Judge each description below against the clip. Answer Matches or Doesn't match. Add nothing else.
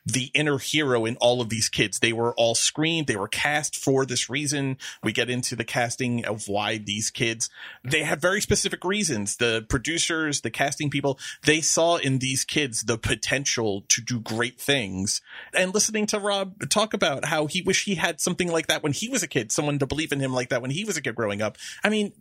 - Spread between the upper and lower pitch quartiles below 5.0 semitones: Doesn't match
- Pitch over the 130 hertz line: Matches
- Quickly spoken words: Matches